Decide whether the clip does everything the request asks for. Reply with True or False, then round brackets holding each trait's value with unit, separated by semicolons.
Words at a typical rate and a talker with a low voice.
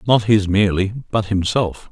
True (155 wpm; 105 Hz)